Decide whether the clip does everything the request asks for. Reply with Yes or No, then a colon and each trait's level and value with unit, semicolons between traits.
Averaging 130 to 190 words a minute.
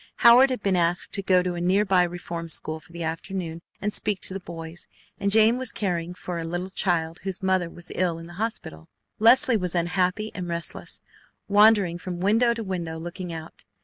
No: average, 200 wpm